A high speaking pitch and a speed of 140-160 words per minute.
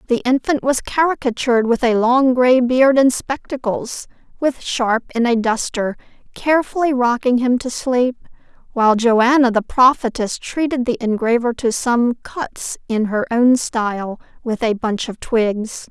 Yes: high, 245 Hz; average, 150 wpm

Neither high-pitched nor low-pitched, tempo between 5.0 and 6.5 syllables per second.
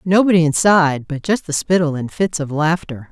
Yes: medium, 165 Hz; 5.3 syllables/s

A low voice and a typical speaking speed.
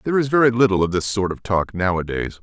No: low, 105 Hz; fast, 295 wpm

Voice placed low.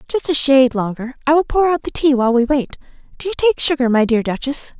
No: very high, 270 Hz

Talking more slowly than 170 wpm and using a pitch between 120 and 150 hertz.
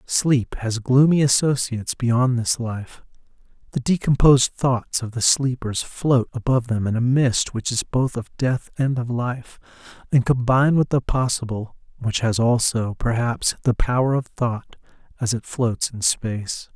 Yes: average, 160 wpm; low, 125 Hz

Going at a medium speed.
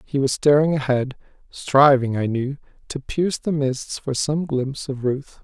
Yes: average, 175 wpm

